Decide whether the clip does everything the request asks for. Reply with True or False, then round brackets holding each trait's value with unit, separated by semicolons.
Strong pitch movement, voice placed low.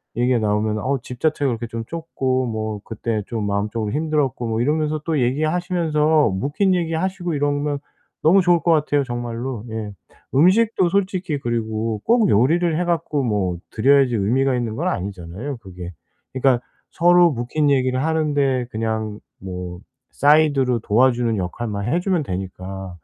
True (6.1 semitones; 130 Hz)